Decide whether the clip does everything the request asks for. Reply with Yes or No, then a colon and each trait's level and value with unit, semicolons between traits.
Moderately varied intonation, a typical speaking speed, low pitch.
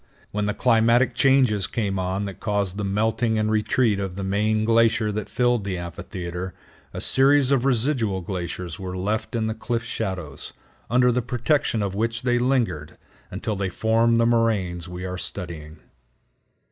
Yes: average, 3.7 semitones; average, 165 wpm; low, 110 Hz